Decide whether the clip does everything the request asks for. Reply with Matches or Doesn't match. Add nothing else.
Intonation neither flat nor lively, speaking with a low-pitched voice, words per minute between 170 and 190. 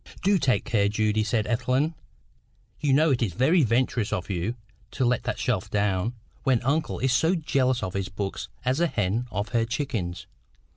Matches